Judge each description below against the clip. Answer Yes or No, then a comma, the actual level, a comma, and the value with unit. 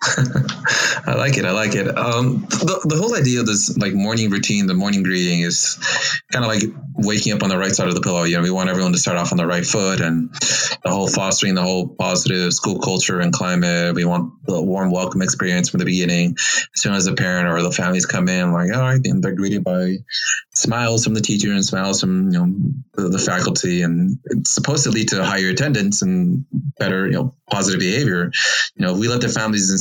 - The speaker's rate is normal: No, fast, 230 wpm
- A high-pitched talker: No, very low, 95 Hz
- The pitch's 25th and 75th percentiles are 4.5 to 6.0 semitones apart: Yes, wide, 5.6 semitones